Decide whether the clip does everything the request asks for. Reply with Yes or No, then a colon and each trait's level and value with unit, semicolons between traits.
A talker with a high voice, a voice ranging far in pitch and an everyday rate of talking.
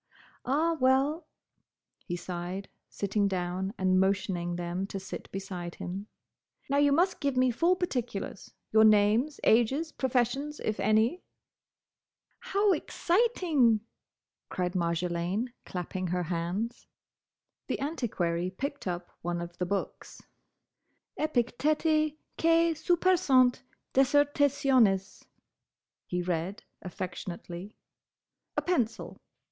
No: high, 220 Hz; wide, 8.0 semitones; slow, 100 wpm